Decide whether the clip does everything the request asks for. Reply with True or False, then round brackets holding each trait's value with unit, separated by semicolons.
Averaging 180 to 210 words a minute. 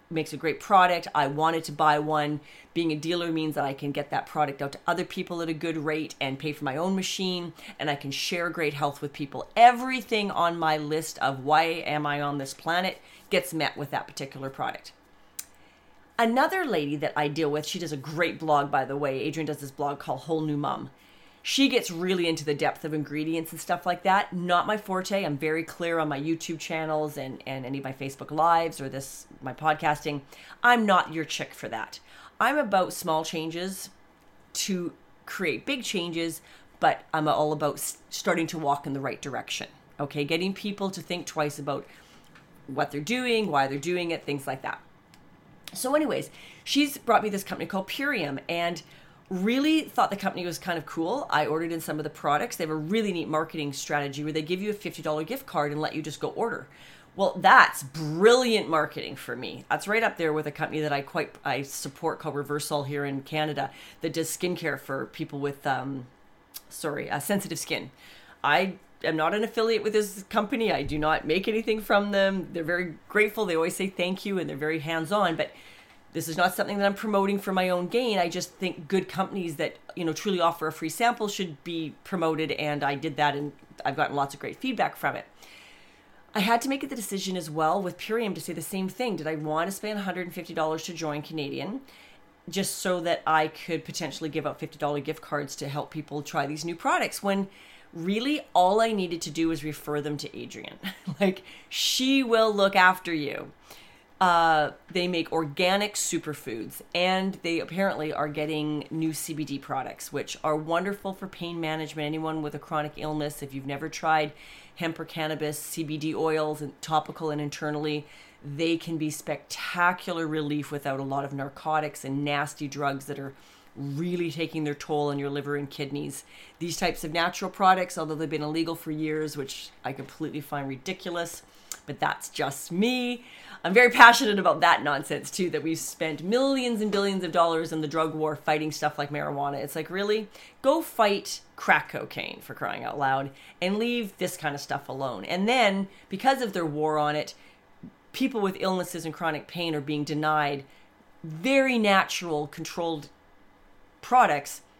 True (195 wpm)